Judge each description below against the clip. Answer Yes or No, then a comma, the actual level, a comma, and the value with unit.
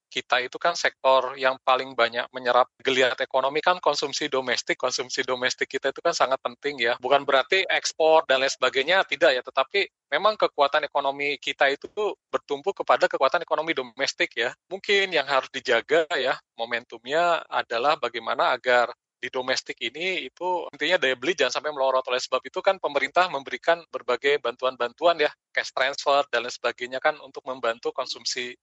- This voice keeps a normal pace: No, fast, 165 wpm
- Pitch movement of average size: Yes, average, 4.2 semitones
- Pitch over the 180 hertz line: No, low, 135 Hz